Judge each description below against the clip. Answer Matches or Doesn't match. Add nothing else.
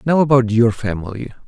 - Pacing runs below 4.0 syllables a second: Doesn't match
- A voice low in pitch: Matches